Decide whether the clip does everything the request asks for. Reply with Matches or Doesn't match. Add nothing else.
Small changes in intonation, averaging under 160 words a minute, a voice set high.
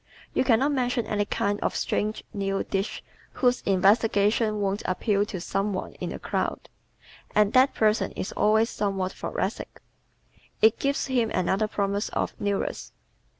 Matches